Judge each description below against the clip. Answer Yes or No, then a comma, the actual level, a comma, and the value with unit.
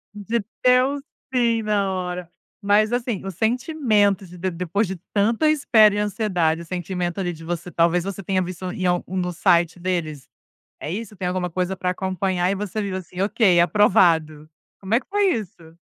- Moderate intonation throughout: Yes, average, 3.2 semitones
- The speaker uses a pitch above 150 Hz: Yes, high, 190 Hz